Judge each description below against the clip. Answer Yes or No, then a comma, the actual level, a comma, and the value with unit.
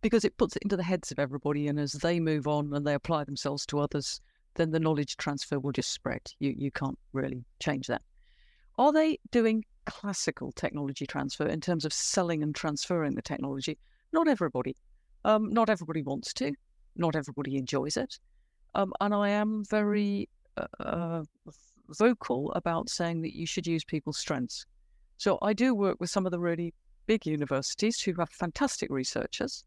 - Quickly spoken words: No, average, 180 wpm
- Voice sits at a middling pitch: Yes, medium, 165 Hz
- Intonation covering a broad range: Yes, wide, 6.1 semitones